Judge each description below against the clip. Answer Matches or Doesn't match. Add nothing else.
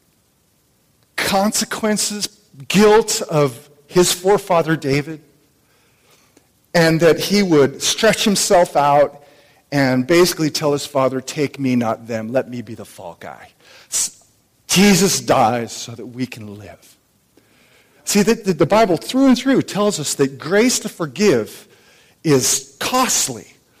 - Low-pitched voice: Doesn't match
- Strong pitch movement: Matches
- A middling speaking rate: Doesn't match